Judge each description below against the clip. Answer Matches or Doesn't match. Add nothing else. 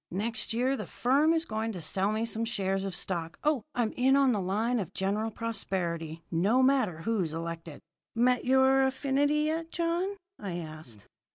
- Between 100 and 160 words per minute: Doesn't match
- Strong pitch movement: Matches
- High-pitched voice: Matches